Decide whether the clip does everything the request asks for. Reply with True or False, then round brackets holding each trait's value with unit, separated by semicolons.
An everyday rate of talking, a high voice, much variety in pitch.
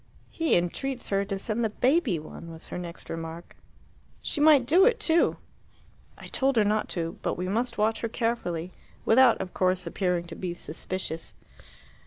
True (175 wpm; 205 Hz; 6.5 semitones)